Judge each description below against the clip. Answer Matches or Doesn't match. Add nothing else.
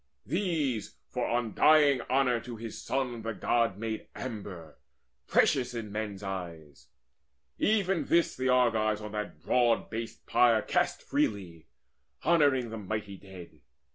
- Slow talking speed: Matches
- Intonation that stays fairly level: Doesn't match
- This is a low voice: Matches